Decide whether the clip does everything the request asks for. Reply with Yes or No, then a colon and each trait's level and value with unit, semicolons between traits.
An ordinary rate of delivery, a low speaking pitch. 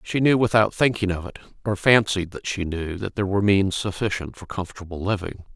Yes: average, 195 wpm; low, 100 Hz